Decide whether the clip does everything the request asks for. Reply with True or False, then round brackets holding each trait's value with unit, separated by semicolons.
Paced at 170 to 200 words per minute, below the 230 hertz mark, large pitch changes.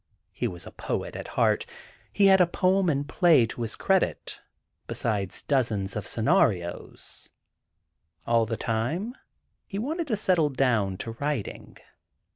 False (145 wpm; 135 Hz; 8.8 semitones)